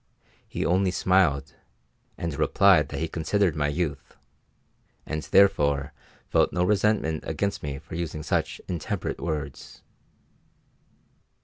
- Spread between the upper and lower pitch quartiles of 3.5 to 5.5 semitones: Yes, average, 3.9 semitones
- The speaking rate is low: Yes, slow, 115 wpm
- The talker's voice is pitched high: No, very low, 80 Hz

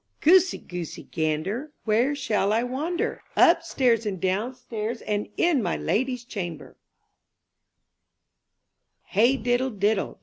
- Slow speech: Yes, slow, 115 wpm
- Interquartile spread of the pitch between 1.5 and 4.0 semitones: No, average, 4.5 semitones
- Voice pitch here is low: No, high, 230 Hz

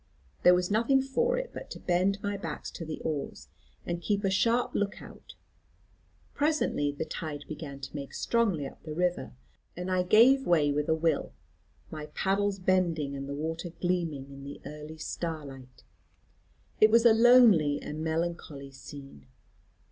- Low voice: No, medium, 170 Hz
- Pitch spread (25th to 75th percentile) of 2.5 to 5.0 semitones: No, wide, 5.5 semitones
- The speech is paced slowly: No, average, 165 wpm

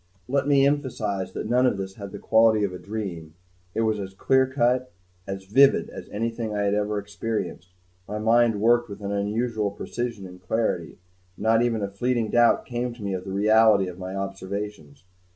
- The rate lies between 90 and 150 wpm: No, average, 190 wpm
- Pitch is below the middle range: Yes, low, 105 Hz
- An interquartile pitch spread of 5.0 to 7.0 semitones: No, average, 3.3 semitones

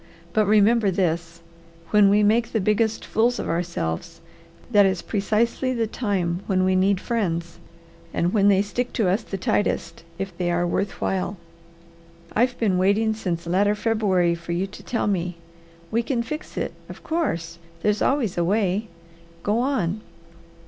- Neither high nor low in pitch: No, high, 200 Hz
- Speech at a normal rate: Yes, average, 160 wpm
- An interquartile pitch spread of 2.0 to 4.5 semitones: Yes, average, 4.0 semitones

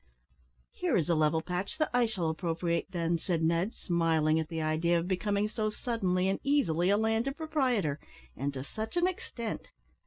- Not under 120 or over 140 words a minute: No, average, 180 wpm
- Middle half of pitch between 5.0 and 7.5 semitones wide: Yes, average, 5.3 semitones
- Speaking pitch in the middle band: Yes, medium, 180 Hz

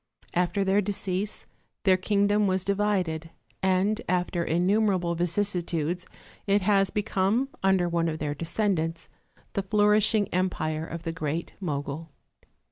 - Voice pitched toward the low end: No, medium, 185 Hz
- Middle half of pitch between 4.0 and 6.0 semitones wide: No, average, 3.3 semitones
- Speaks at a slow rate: Yes, slow, 125 wpm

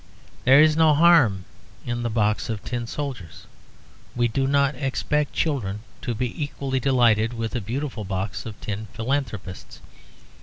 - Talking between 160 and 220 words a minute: No, average, 150 wpm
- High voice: No, low, 120 Hz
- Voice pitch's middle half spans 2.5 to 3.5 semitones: No, average, 4.5 semitones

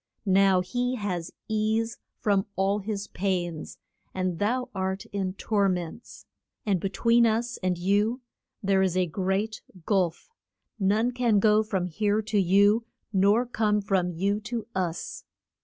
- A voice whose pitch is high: Yes, high, 200 Hz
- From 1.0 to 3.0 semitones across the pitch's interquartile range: Yes, narrow, 2.6 semitones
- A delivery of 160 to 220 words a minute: No, average, 145 wpm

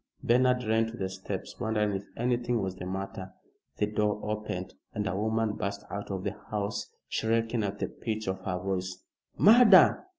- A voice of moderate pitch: No, low, 105 Hz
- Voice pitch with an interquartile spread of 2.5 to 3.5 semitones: Yes, average, 2.8 semitones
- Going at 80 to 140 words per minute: No, average, 175 wpm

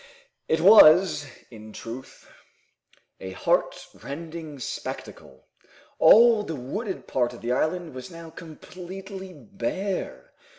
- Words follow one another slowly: Yes, slow, 110 wpm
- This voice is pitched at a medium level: Yes, medium, 165 Hz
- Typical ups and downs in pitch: No, wide, 6.5 semitones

